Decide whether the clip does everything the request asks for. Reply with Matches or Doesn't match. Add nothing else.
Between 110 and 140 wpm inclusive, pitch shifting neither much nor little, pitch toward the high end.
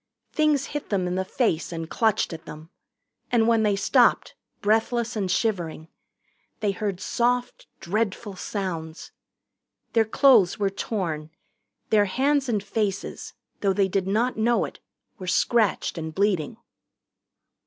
Matches